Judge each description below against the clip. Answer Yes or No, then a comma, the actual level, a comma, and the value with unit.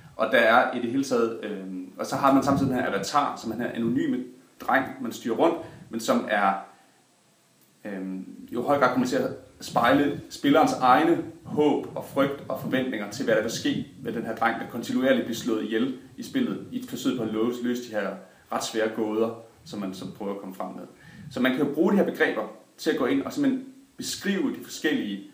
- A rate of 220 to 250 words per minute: Yes, fast, 225 wpm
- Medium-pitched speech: No, low, 120 Hz